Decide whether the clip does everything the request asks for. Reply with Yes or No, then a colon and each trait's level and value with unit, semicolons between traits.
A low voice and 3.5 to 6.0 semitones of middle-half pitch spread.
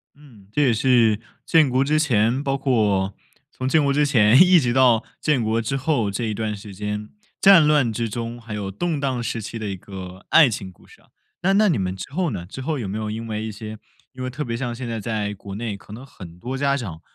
Yes: low, 115 Hz; average, 4.6 semitones